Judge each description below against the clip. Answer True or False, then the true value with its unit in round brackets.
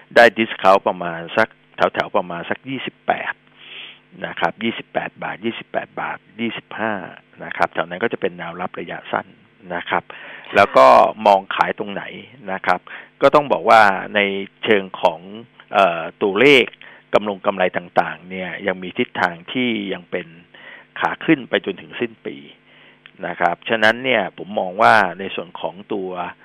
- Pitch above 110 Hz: False (95 Hz)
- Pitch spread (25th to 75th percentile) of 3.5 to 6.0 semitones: True (3.8 semitones)